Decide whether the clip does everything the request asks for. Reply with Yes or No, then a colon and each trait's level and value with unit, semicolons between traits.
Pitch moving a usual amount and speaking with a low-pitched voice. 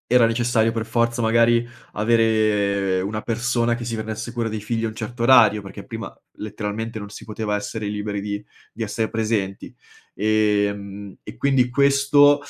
No: narrow, 2.2 semitones; low, 110 Hz